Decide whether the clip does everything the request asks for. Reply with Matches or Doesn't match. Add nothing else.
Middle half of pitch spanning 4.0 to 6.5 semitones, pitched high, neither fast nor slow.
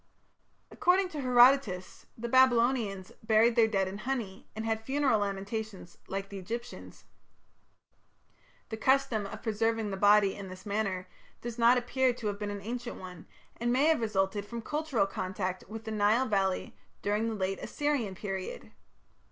Doesn't match